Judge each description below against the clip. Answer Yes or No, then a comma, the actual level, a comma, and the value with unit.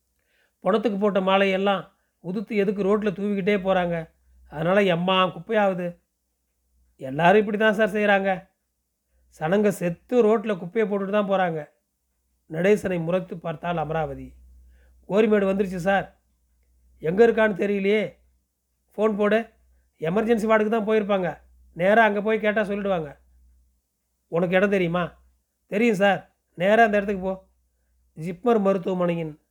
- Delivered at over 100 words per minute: Yes, average, 110 wpm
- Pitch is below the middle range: No, medium, 185 Hz